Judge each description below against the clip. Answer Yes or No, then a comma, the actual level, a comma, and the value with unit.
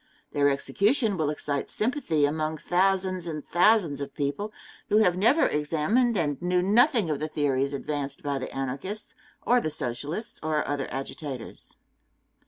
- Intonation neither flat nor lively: No, wide, 5.8 semitones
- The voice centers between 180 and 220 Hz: No, medium, 155 Hz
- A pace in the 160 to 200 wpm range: No, average, 150 wpm